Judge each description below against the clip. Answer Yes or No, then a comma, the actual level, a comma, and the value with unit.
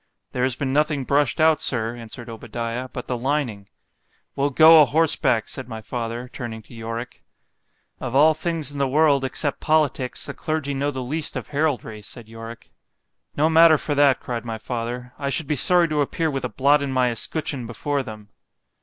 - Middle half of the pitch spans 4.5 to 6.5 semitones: No, average, 3.9 semitones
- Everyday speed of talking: Yes, average, 180 wpm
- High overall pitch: No, low, 130 Hz